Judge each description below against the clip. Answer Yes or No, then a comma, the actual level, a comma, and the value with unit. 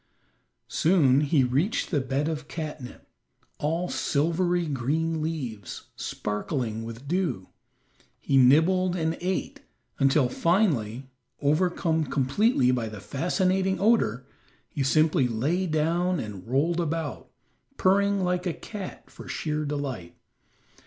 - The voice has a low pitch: No, medium, 155 Hz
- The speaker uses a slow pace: Yes, slow, 115 wpm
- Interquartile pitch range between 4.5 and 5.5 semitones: Yes, average, 5.1 semitones